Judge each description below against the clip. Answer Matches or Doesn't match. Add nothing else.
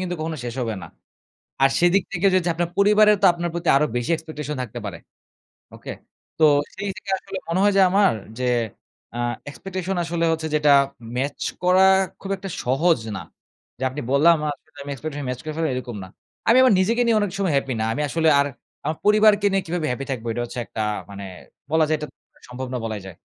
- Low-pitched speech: Doesn't match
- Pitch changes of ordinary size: Doesn't match